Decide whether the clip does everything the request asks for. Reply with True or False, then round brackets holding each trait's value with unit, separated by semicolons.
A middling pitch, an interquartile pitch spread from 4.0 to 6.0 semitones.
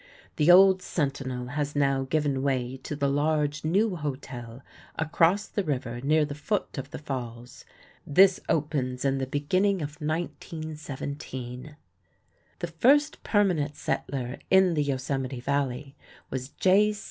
False (145 Hz; 3.6 semitones)